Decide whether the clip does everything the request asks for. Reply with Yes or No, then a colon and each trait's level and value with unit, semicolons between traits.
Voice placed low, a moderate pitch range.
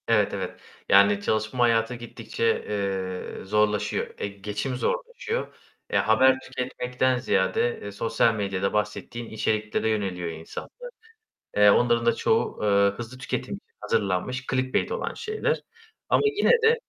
Yes: low, 115 Hz; average, 4.1 semitones